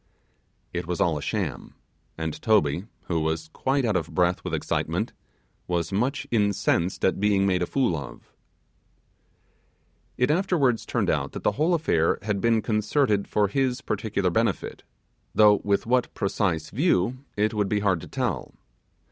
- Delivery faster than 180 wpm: No, average, 155 wpm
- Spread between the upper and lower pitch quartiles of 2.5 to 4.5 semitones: No, average, 5.3 semitones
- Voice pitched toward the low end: Yes, low, 105 Hz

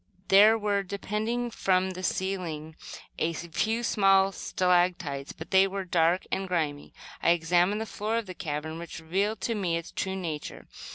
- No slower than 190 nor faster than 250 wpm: No, average, 165 wpm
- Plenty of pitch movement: No, average, 3.2 semitones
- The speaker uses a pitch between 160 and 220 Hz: Yes, medium, 185 Hz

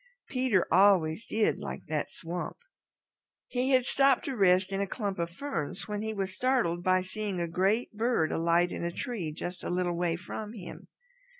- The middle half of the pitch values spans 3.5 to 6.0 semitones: Yes, average, 4.3 semitones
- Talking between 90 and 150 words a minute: No, average, 185 wpm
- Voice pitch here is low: No, high, 190 Hz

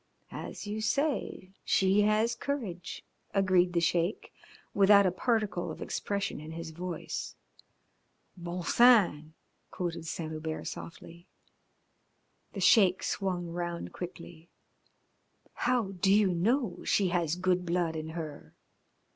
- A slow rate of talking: Yes, slow, 120 wpm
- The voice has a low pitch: No, medium, 180 Hz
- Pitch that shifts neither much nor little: Yes, average, 3.1 semitones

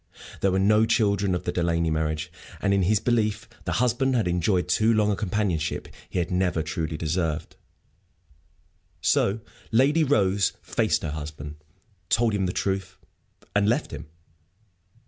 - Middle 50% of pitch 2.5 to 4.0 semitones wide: No, average, 4.4 semitones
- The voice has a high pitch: No, very low, 95 Hz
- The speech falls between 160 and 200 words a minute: No, average, 150 wpm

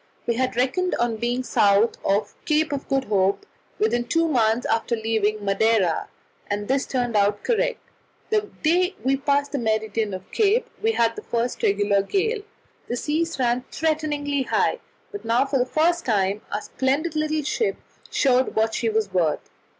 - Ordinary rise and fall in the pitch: No, wide, 5.9 semitones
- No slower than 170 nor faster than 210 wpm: Yes, average, 175 wpm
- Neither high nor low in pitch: No, high, 245 Hz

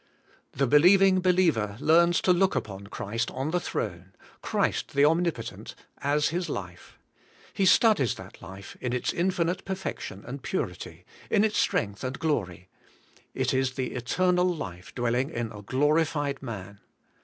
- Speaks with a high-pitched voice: No, medium, 140 Hz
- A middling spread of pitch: No, wide, 7.8 semitones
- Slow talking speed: No, average, 145 wpm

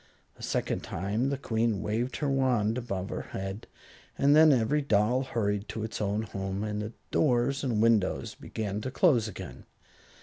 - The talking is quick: No, average, 170 wpm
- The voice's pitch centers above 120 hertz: No, low, 110 Hz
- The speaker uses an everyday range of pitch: Yes, average, 4.0 semitones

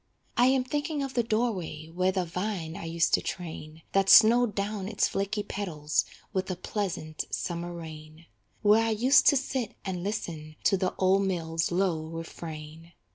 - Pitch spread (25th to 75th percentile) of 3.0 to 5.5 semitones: Yes, average, 4.6 semitones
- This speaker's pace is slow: No, average, 175 wpm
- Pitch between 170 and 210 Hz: Yes, medium, 185 Hz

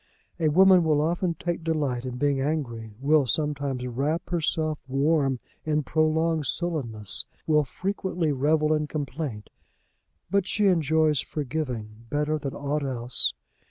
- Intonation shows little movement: No, average, 3.0 semitones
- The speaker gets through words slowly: Yes, slow, 130 wpm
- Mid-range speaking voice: Yes, medium, 150 Hz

